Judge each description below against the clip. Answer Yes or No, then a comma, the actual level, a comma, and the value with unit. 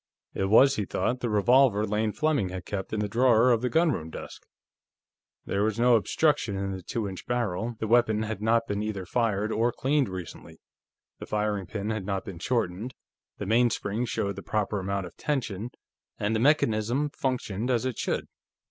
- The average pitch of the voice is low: Yes, low, 110 Hz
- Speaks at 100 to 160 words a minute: No, average, 185 wpm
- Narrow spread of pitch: No, average, 3.5 semitones